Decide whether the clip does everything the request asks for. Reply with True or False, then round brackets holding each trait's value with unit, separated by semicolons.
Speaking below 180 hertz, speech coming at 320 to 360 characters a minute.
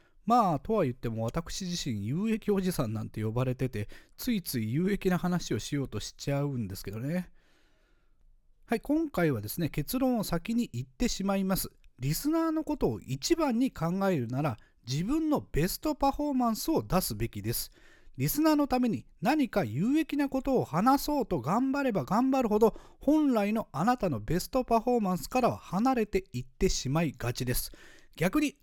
False (190 Hz; 355 characters per minute)